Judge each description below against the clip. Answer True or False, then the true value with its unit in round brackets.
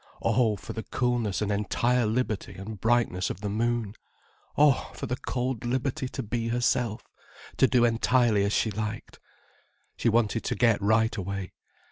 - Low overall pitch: True (115 Hz)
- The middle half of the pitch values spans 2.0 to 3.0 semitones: True (2.7 semitones)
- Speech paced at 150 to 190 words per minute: True (160 wpm)